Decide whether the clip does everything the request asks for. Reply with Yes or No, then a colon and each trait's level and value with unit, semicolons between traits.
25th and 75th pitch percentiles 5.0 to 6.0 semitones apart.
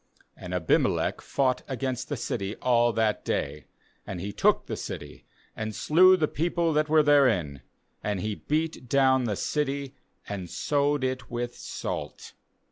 Yes: wide, 5.6 semitones